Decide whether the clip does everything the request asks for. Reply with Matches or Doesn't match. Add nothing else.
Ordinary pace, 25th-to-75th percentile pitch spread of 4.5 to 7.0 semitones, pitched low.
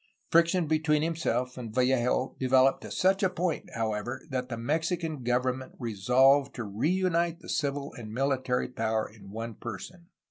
Matches